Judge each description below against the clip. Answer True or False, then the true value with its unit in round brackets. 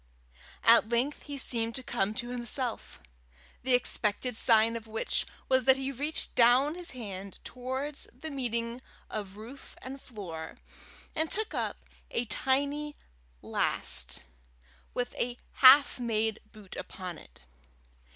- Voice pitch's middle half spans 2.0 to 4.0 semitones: True (3.4 semitones)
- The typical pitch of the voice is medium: False (245 Hz)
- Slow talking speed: True (130 wpm)